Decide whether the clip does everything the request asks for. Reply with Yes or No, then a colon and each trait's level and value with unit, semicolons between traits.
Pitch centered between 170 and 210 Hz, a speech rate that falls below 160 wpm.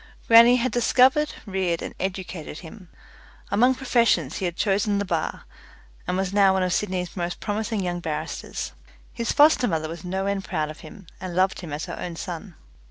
No: high, 190 Hz; average, 185 wpm